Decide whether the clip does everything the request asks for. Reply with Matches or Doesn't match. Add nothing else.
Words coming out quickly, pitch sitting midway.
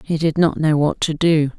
Matches